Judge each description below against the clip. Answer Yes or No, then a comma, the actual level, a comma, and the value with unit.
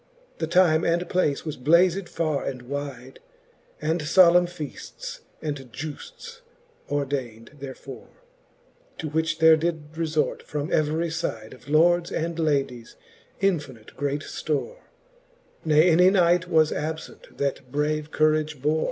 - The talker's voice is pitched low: No, medium, 155 Hz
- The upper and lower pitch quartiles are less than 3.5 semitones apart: Yes, average, 2.9 semitones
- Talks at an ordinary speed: No, slow, 130 wpm